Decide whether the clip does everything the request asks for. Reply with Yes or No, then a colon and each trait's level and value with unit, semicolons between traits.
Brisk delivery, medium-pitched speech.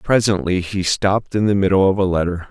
No: fast, 215 wpm; very low, 95 Hz